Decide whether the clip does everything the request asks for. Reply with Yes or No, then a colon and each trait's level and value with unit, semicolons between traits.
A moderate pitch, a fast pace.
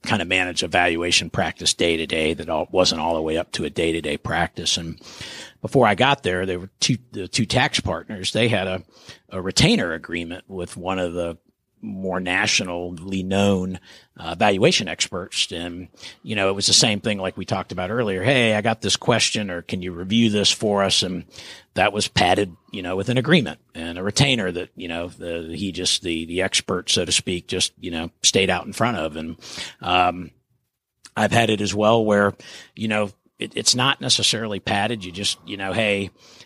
No: very low, 95 Hz; fast, 210 wpm